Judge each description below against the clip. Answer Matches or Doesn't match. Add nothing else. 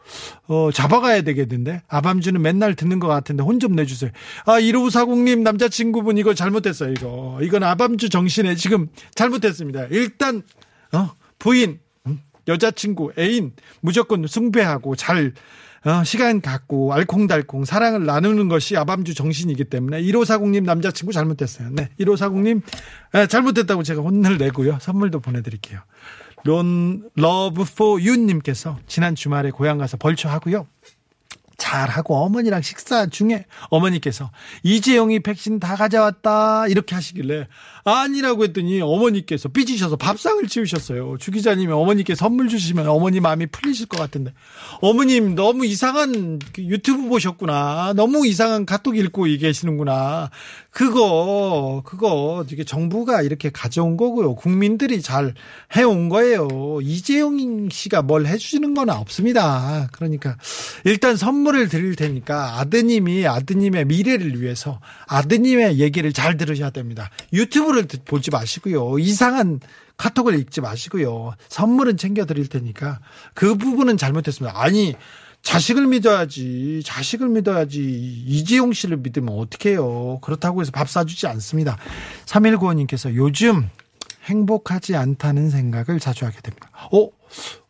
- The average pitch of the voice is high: Doesn't match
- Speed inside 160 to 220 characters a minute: Doesn't match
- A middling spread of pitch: Doesn't match